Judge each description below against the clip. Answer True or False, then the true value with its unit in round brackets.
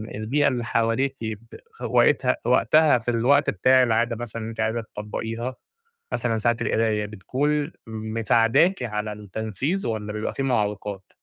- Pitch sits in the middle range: False (115 Hz)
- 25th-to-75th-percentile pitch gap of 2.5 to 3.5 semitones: True (2.8 semitones)